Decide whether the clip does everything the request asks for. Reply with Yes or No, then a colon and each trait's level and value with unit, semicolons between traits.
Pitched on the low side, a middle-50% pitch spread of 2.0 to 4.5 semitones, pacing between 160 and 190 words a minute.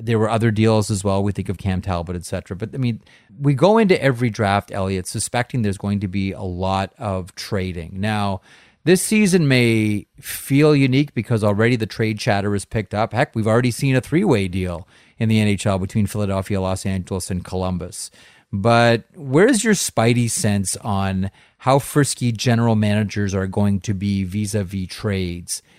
Yes: low, 105 Hz; average, 3.6 semitones; average, 180 wpm